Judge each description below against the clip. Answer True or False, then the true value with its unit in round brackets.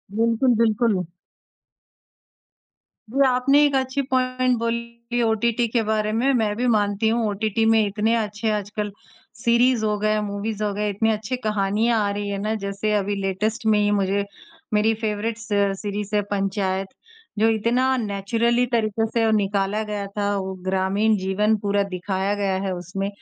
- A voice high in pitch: True (215 Hz)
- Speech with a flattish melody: True (2.3 semitones)